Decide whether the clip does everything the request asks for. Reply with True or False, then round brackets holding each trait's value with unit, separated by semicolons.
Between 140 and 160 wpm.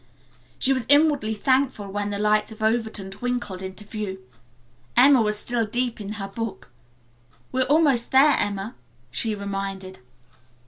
True (145 wpm)